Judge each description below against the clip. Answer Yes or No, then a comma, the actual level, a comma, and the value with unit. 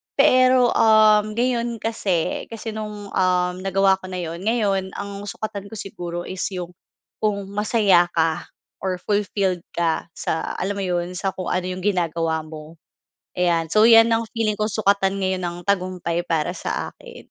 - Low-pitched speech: No, high, 195 Hz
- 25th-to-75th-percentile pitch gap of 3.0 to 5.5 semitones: Yes, average, 3.3 semitones